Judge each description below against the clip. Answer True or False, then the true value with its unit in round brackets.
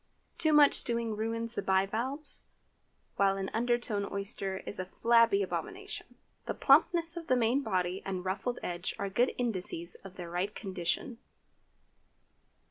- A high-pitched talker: True (215 Hz)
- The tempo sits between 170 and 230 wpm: False (140 wpm)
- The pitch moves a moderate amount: True (4.2 semitones)